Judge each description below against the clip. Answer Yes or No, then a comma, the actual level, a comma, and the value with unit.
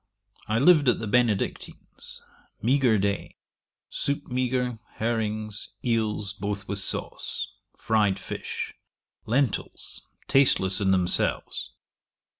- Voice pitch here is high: No, low, 110 Hz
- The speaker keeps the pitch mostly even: No, average, 3.6 semitones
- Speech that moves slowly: Yes, slow, 95 wpm